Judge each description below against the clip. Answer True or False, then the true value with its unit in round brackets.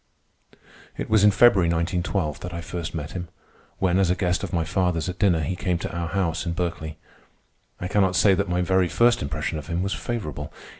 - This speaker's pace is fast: True (210 wpm)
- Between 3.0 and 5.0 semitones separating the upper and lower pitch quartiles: False (2.4 semitones)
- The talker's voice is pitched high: False (90 Hz)